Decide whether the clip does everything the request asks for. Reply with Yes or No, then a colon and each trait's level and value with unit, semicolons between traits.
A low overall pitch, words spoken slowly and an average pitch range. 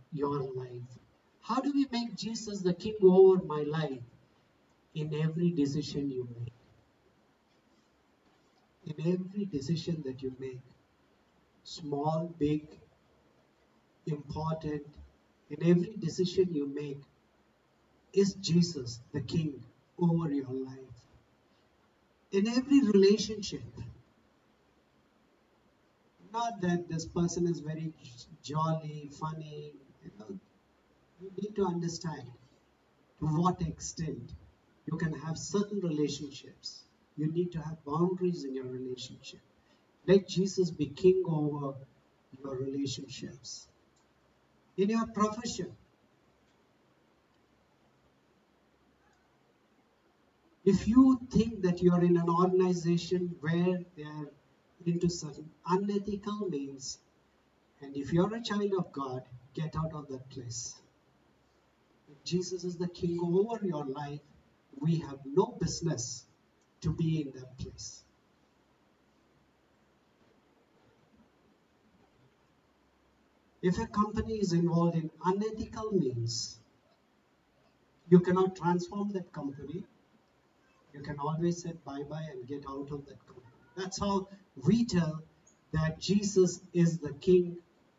No: medium, 160 Hz; slow, 110 wpm; average, 4.9 semitones